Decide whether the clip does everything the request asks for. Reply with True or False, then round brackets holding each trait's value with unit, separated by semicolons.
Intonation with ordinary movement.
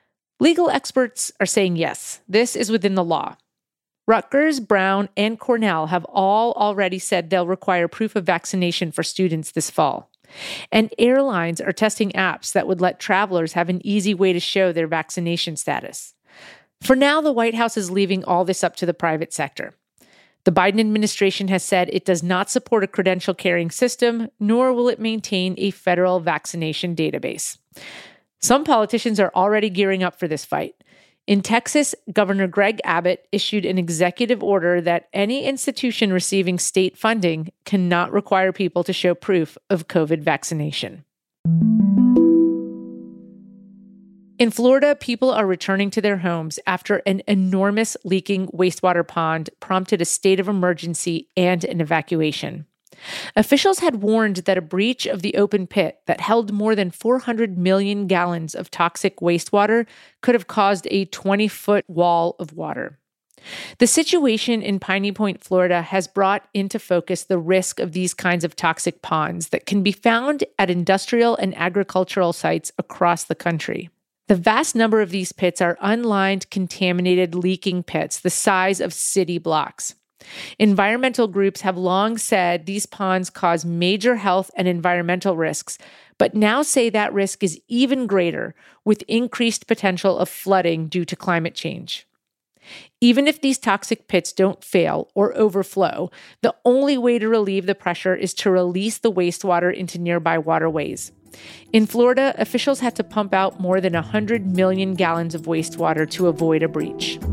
True (3.4 semitones)